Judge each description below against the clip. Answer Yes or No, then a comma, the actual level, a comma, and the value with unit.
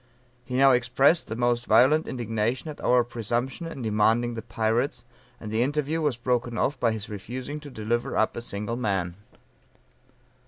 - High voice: No, low, 120 Hz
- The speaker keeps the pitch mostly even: No, average, 3.0 semitones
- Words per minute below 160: No, average, 165 wpm